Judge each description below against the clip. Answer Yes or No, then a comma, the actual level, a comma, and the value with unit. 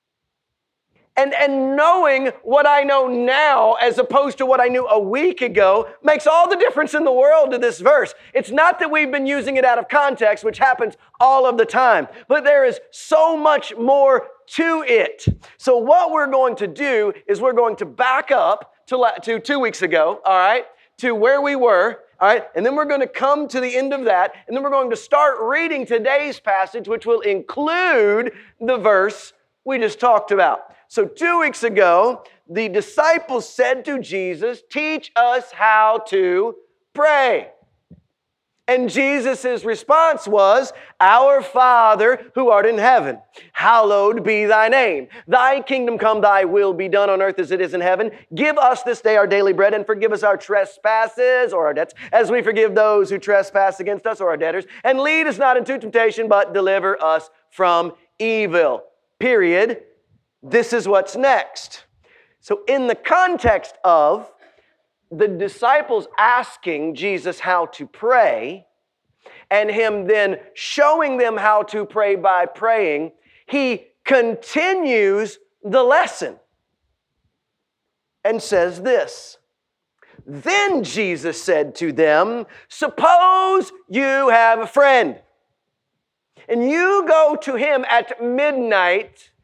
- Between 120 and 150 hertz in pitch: No, very high, 250 Hz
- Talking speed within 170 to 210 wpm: No, average, 155 wpm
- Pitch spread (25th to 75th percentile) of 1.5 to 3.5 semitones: No, wide, 5.5 semitones